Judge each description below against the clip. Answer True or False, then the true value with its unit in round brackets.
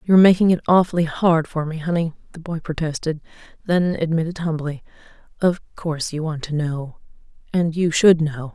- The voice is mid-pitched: True (160 Hz)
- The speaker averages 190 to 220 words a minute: False (170 wpm)